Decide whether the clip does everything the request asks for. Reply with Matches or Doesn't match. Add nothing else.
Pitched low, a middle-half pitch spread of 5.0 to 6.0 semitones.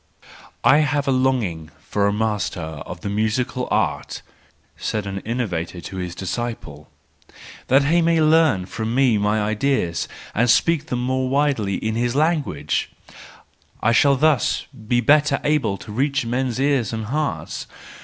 Matches